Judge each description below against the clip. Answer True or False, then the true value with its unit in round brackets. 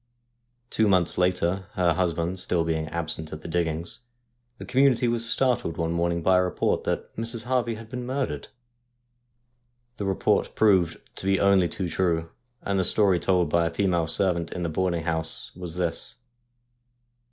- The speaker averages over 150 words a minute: True (170 wpm)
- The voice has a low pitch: True (90 Hz)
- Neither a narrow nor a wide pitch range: True (3.1 semitones)